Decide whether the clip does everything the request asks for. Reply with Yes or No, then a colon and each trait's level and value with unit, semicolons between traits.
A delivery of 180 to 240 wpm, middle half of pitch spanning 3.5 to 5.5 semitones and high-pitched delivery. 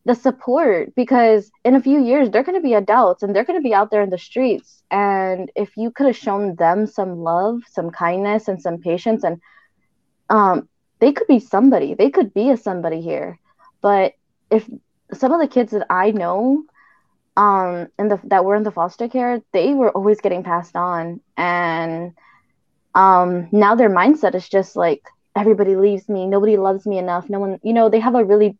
Yes: average, 195 wpm; average, 4.2 semitones; high, 205 Hz